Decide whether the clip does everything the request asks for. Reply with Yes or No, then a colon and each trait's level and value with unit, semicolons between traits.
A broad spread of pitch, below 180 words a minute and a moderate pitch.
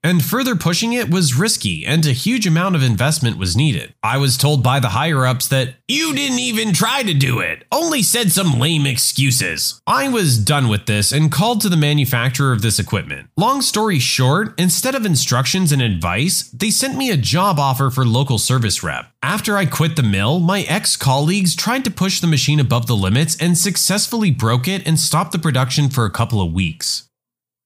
No: wide, 6.7 semitones; fast, 205 wpm; medium, 150 Hz